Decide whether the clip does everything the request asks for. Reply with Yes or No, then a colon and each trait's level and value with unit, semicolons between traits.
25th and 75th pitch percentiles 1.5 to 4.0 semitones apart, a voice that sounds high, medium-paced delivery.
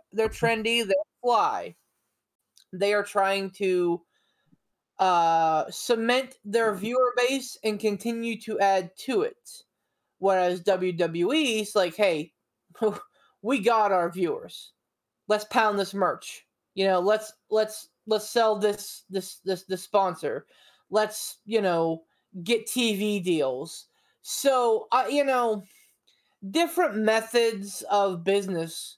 No: average, 3.5 semitones; high, 215 Hz; slow, 120 wpm